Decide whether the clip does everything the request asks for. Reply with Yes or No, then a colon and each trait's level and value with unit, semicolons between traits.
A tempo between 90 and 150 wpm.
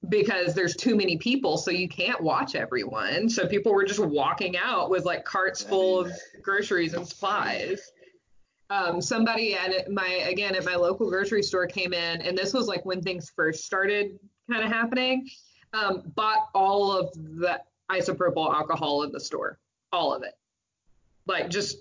No: average, 170 wpm